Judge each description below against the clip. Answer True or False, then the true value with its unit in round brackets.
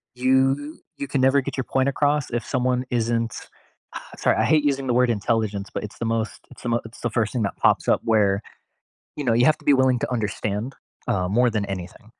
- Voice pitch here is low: True (120 Hz)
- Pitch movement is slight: False (3.2 semitones)